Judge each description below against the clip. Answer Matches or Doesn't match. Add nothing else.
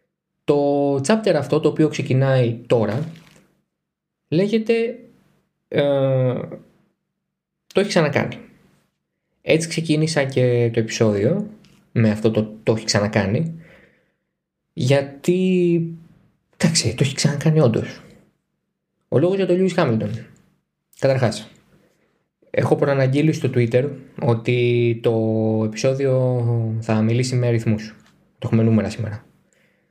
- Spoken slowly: Matches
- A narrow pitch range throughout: Doesn't match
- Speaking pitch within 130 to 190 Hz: Matches